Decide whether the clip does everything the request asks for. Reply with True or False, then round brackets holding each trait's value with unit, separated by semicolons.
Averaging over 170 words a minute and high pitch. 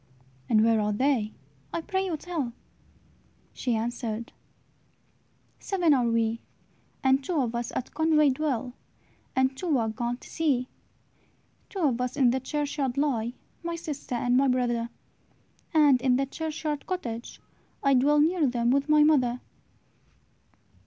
False (145 wpm; 265 Hz)